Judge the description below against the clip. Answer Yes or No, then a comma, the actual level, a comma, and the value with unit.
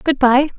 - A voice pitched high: Yes, very high, 270 Hz